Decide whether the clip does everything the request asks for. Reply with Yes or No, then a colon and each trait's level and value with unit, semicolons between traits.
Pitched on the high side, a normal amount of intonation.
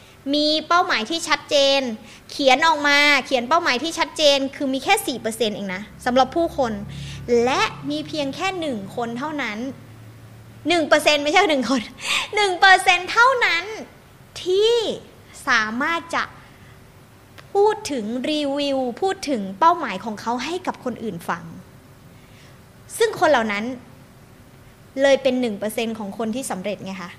No: very high, 275 Hz; wide, 6.5 semitones